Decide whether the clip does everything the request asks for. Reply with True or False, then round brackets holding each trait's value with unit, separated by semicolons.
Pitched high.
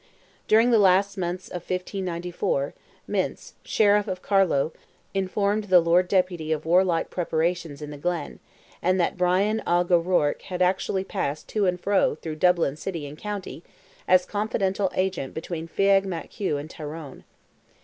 False (180 Hz)